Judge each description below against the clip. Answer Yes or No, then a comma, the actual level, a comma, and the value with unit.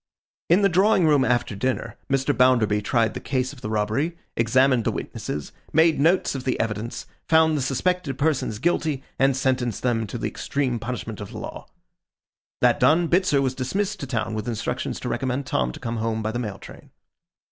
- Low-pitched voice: Yes, low, 130 Hz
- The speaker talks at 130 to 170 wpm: No, average, 190 wpm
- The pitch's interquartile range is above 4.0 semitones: Yes, average, 4.7 semitones